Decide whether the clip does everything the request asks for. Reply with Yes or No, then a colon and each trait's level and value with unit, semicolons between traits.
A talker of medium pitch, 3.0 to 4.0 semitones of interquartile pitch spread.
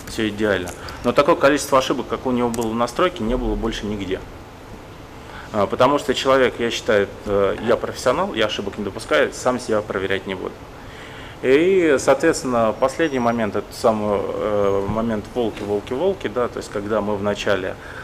No: low, 115 Hz; average, 3.7 semitones